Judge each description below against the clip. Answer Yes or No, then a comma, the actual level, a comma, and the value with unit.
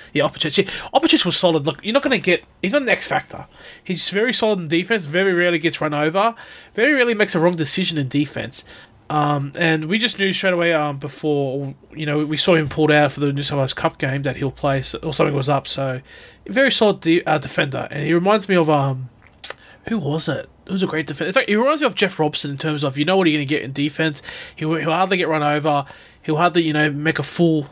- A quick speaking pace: Yes, fast, 250 wpm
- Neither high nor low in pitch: Yes, medium, 160 Hz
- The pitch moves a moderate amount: Yes, average, 4.2 semitones